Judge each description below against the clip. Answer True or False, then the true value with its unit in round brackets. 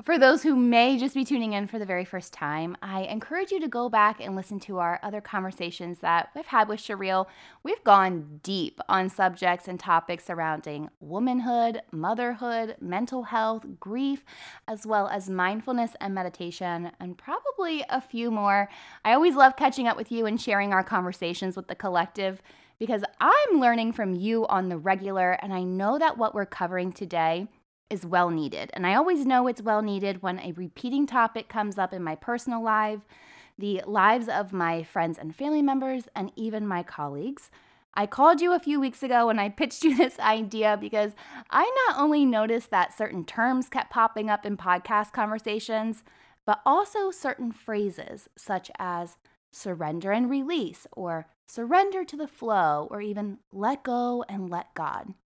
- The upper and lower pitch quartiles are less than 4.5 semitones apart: False (5.1 semitones)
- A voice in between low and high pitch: False (215 Hz)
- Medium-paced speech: True (180 wpm)